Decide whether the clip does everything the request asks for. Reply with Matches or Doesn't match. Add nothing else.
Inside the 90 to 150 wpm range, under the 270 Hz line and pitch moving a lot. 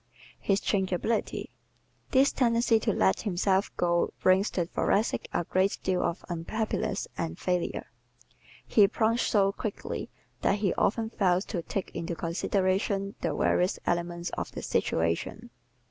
Doesn't match